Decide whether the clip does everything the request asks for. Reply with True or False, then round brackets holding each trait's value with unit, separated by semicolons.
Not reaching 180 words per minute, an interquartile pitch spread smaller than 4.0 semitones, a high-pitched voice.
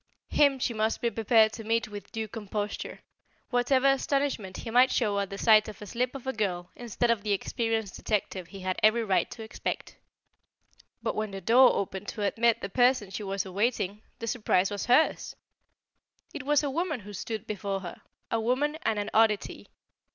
False (195 wpm; 3.3 semitones; 220 Hz)